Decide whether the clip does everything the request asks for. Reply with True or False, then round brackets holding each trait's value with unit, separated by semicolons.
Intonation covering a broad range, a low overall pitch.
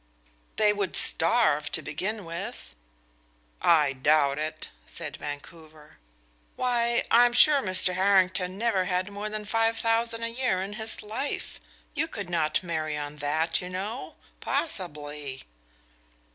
False (6.5 semitones; 185 Hz)